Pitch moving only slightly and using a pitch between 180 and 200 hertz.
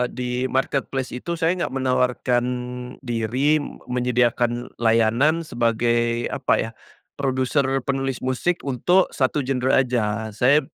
No: narrow, 2.3 semitones; low, 125 Hz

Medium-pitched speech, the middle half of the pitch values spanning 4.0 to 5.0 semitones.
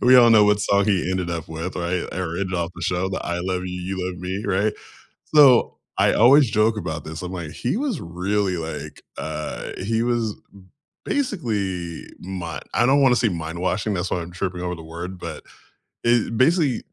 No: very low, 95 Hz; average, 4.5 semitones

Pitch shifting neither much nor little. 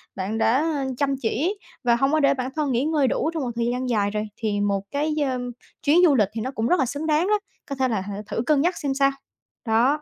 Yes: average, 4.6 semitones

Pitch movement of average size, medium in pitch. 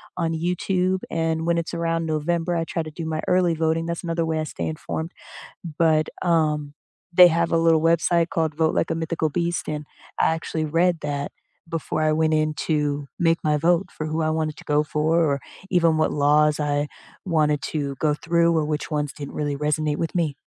No: narrow, 1.7 semitones; medium, 160 Hz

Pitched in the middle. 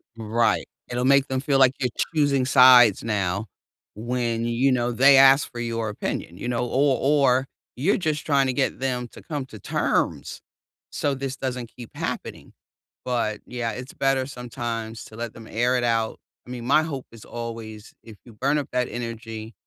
No: low, 125 Hz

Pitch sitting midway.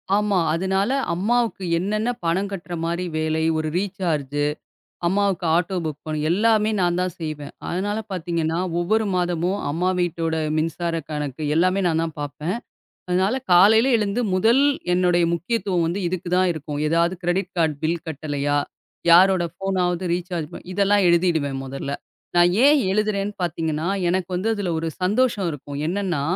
Yes: medium, 175 Hz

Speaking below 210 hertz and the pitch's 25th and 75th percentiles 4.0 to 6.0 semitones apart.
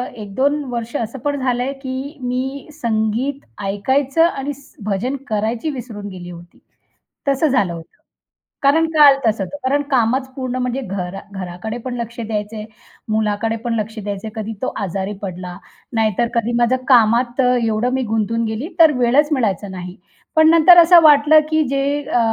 No: high, 240 Hz; average, 4.5 semitones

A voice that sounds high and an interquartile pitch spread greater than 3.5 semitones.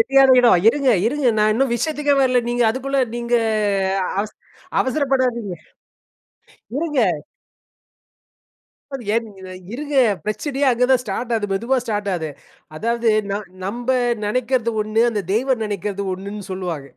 Yes: high, 235 Hz; average, 4.1 semitones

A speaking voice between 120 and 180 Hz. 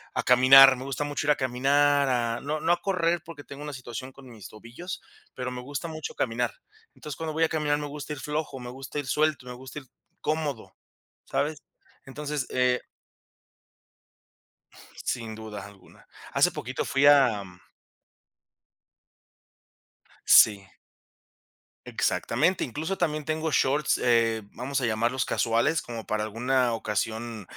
Yes: low, 135 Hz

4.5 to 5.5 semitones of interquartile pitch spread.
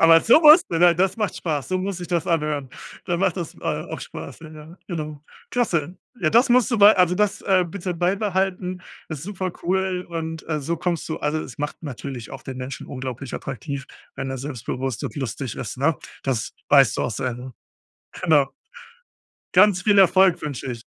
Yes: average, 5.1 semitones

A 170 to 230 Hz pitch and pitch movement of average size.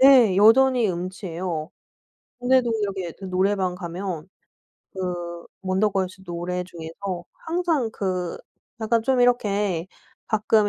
Yes: high, 190 Hz; average, 3.8 semitones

